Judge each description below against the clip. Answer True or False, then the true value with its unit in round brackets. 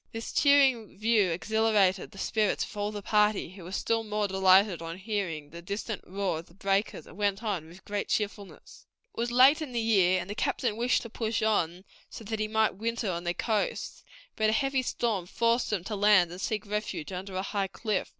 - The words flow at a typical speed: False (215 wpm)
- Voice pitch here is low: False (205 Hz)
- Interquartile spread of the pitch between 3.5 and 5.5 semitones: False (2.9 semitones)